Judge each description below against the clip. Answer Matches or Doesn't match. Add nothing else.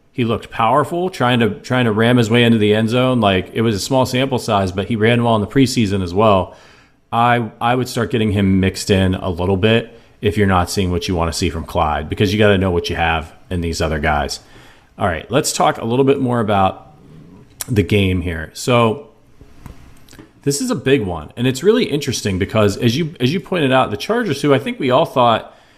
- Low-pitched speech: Matches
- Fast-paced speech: Matches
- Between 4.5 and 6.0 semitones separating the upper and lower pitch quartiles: Matches